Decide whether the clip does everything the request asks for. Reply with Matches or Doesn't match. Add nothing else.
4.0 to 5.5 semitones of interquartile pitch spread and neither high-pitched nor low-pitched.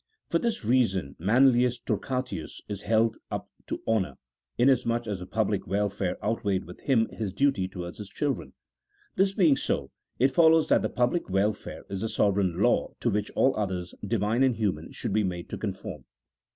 Doesn't match